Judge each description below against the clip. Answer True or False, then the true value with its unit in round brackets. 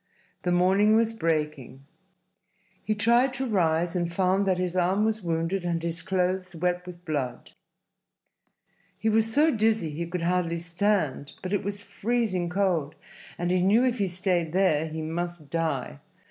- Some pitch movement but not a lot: True (3.4 semitones)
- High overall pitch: False (180 Hz)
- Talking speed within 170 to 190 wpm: False (160 wpm)